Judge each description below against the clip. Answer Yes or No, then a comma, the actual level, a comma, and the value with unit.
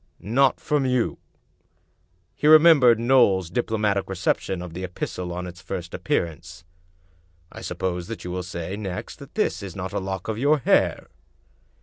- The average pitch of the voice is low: Yes, very low, 95 Hz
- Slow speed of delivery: No, average, 165 wpm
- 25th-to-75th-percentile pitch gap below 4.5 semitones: No, average, 4.8 semitones